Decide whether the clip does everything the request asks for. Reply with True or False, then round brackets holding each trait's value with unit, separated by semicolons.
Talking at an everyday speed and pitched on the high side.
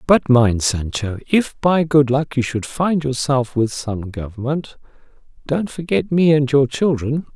False (165 wpm; 140 Hz)